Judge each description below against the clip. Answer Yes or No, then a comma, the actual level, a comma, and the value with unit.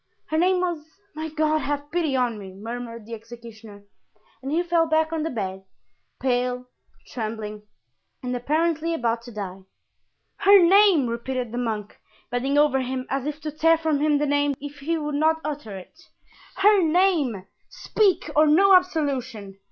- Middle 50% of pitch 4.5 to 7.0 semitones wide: Yes, average, 5.3 semitones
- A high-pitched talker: Yes, very high, 285 Hz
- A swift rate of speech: No, average, 160 wpm